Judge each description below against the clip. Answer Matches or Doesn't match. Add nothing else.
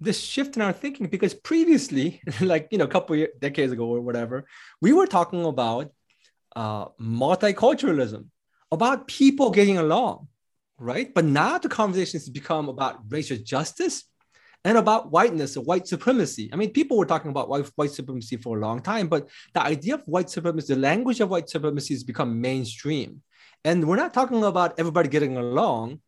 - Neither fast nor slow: Matches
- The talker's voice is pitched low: Doesn't match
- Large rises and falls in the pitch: Matches